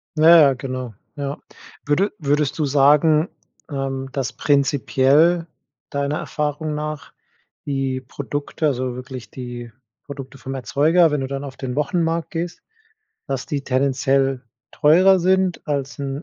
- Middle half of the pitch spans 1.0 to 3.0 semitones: Yes, narrow, 2.4 semitones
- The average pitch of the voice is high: No, medium, 140 Hz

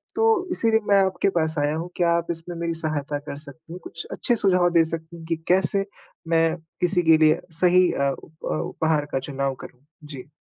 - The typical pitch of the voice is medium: Yes, medium, 165 Hz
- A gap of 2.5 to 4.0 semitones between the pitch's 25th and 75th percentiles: Yes, average, 2.9 semitones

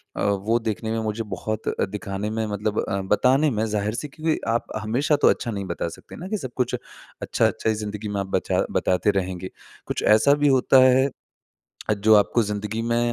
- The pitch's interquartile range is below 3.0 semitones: No, average, 3.3 semitones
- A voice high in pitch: No, low, 110 Hz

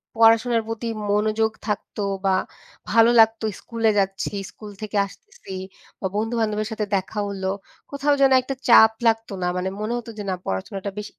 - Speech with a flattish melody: Yes, narrow, 1.9 semitones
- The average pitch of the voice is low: No, high, 220 Hz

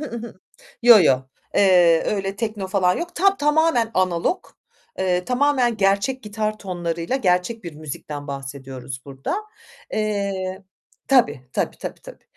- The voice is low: No, high, 195 Hz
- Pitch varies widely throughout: Yes, wide, 5.8 semitones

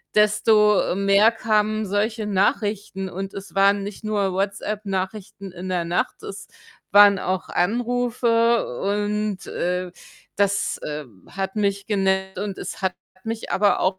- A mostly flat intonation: Yes, narrow, 1.9 semitones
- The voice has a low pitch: No, high, 200 Hz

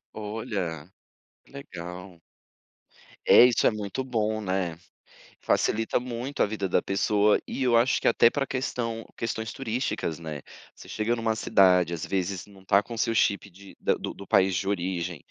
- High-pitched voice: No, low, 105 Hz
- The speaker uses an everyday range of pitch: Yes, average, 3.9 semitones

